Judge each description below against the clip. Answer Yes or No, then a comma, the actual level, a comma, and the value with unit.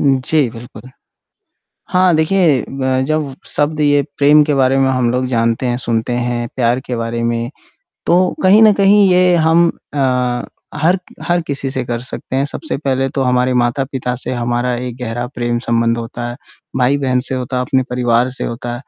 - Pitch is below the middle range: Yes, low, 130 Hz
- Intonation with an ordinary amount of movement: Yes, average, 3.3 semitones